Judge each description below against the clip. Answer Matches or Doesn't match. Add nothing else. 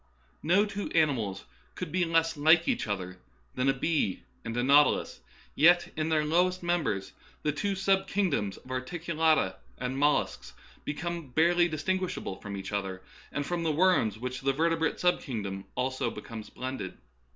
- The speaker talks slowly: Doesn't match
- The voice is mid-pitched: Matches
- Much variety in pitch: Matches